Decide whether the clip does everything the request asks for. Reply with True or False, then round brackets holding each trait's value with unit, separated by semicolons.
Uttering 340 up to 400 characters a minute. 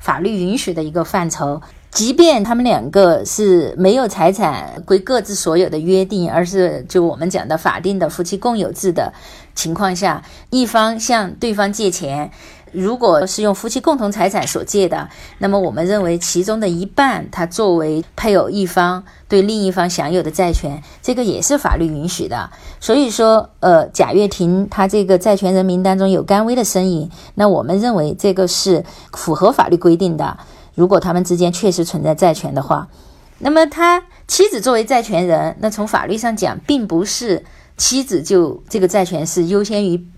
False (275 characters per minute)